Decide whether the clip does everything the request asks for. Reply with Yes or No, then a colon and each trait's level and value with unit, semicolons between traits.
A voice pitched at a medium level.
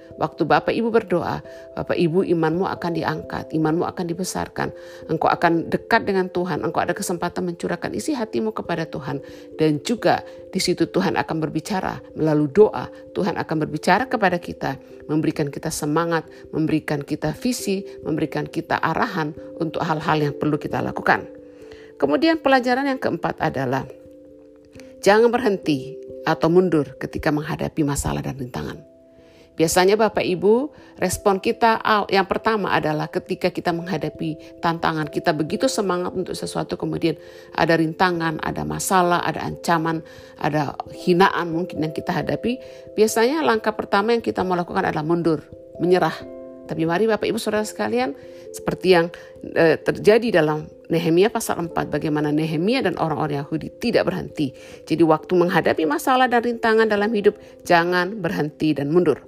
Yes: medium, 170 Hz